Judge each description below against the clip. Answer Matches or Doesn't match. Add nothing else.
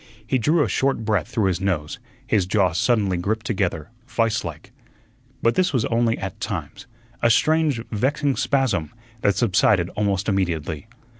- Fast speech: Doesn't match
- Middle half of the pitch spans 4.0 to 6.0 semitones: Matches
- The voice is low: Matches